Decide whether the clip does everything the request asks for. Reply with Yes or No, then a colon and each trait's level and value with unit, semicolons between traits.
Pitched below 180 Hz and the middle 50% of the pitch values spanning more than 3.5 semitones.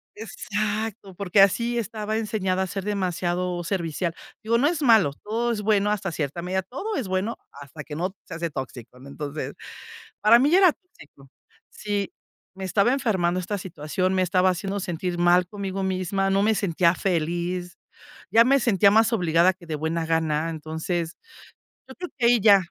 No: high, 190 Hz; average, 3.9 semitones